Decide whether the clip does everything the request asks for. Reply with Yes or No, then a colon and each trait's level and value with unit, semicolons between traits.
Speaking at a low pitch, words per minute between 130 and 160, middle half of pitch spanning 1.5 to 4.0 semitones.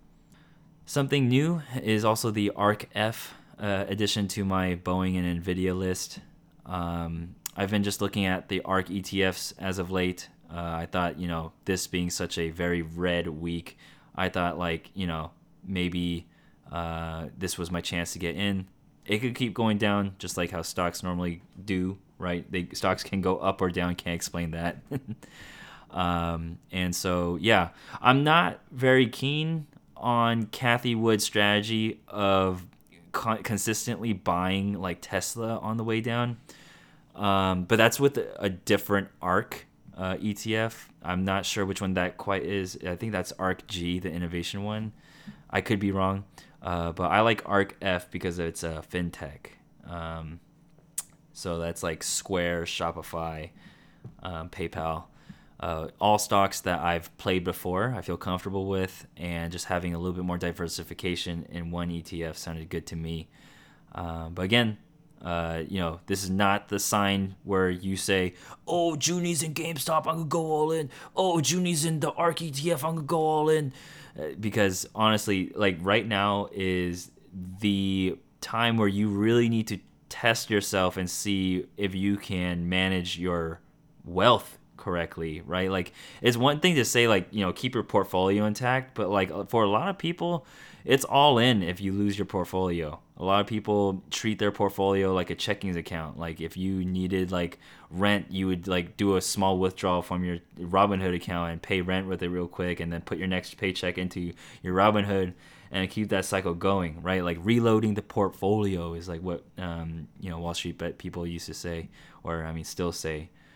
No: very low, 95 Hz; average, 175 wpm; average, 3.3 semitones